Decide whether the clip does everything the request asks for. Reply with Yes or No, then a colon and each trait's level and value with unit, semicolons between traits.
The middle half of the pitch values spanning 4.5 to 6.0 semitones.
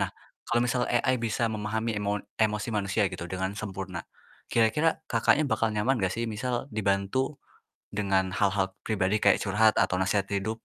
No: average, 2.7 semitones